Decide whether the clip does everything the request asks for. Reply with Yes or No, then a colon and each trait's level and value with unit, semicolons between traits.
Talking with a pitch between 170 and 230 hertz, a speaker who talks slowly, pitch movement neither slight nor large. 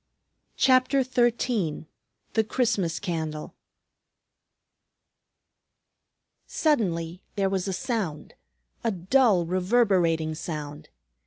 No: high, 190 Hz; slow, 75 wpm; wide, 6.4 semitones